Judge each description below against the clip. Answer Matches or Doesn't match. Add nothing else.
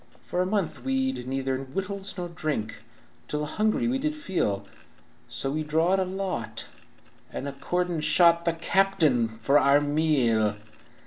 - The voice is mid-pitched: Matches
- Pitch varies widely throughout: Matches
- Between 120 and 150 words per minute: Matches